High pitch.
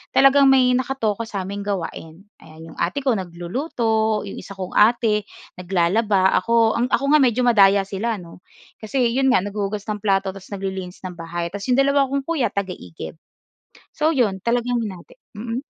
Yes: high, 210 Hz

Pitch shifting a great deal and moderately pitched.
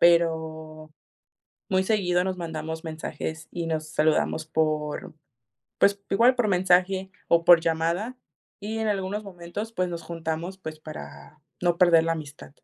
No: average, 3.0 semitones; medium, 170 Hz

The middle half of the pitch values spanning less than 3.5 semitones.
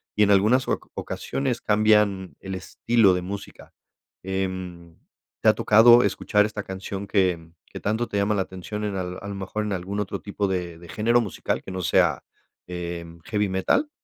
Yes: narrow, 2.4 semitones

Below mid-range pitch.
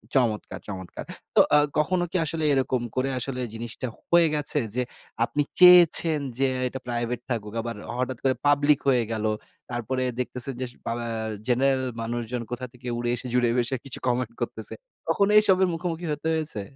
Yes: low, 130 Hz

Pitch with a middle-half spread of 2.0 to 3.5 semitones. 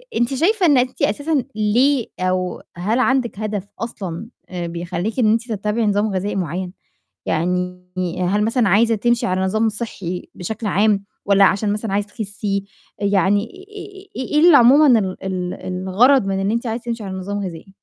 No: average, 4.0 semitones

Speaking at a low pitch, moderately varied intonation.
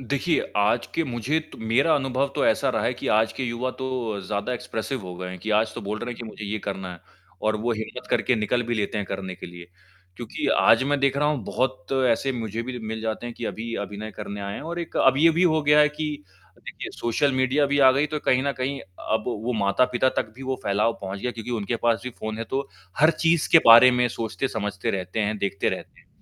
Yes: low, 120 Hz; average, 3.9 semitones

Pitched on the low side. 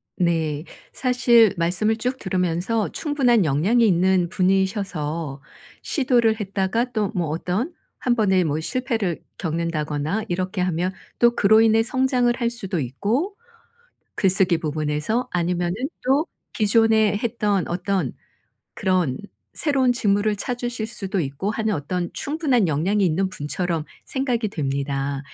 No: high, 195 Hz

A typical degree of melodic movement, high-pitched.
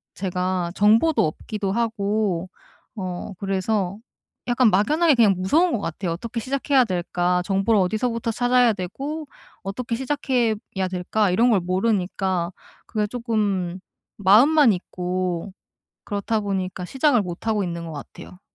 Yes: average, 4.3 semitones; high, 205 Hz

